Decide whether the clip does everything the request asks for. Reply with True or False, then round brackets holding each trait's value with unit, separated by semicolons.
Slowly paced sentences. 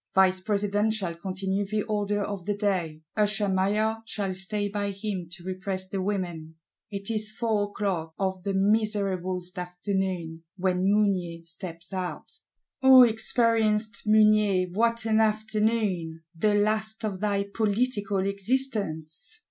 True (130 wpm)